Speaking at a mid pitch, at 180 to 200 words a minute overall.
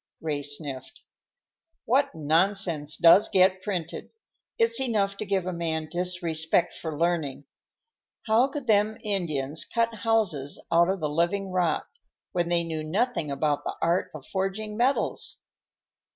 No: medium, 175 Hz; slow, 135 wpm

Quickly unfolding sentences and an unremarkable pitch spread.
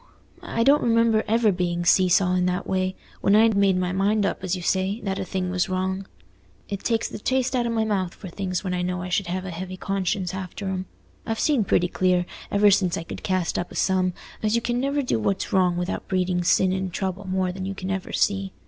No: fast, 240 wpm; narrow, 2.1 semitones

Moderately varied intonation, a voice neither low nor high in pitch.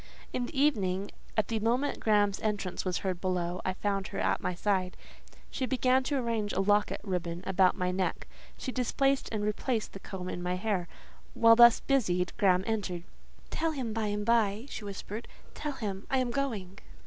No: average, 4.2 semitones; high, 205 Hz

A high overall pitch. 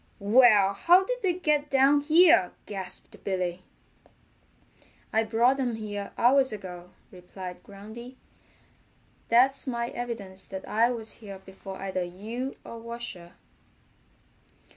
Yes: high, 225 Hz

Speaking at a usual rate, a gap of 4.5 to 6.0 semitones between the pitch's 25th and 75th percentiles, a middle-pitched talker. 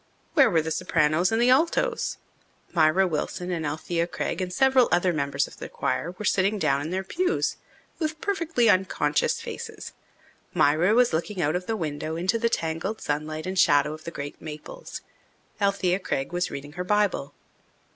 Yes: average, 175 wpm; wide, 5.5 semitones; medium, 180 Hz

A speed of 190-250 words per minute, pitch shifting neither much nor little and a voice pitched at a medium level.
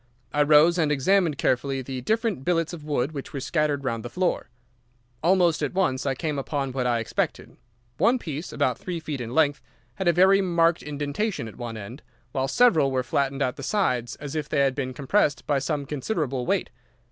Yes: average, 200 wpm; average, 4.3 semitones; medium, 145 Hz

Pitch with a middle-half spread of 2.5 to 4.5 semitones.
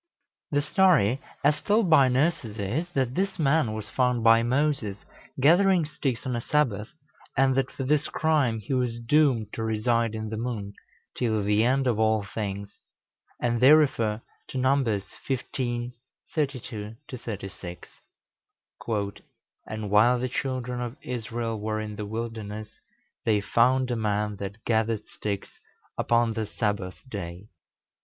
Yes: average, 3.8 semitones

